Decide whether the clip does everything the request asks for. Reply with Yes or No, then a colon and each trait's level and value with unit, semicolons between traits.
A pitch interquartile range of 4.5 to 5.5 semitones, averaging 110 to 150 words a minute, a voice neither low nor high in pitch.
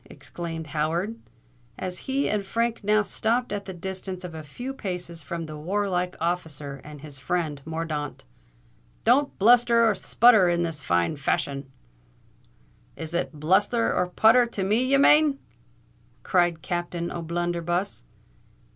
Yes: average, 4.8 semitones; average, 140 wpm; medium, 175 Hz